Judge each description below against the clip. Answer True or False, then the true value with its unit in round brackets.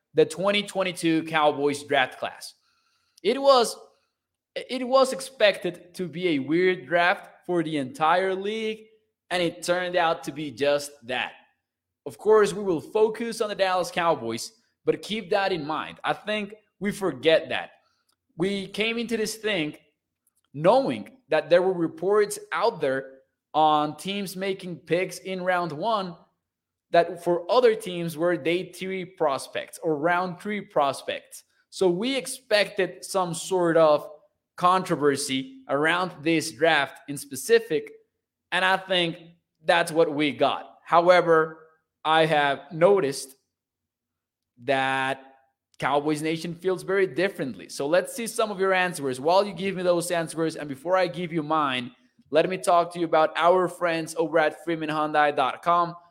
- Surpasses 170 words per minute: False (145 wpm)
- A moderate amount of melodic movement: True (3.8 semitones)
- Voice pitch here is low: False (175 Hz)